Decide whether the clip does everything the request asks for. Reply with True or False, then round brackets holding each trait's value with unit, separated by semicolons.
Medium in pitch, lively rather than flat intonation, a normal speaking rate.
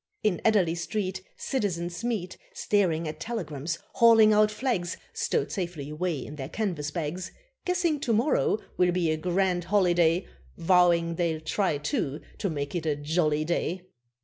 False (175 Hz; 4.7 semitones; 150 wpm)